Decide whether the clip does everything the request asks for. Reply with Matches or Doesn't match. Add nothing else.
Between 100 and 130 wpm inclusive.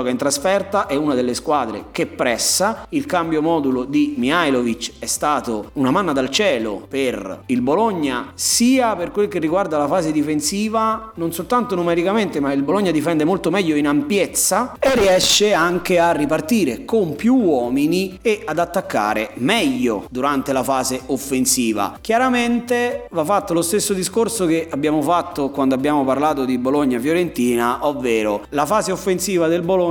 Doesn't match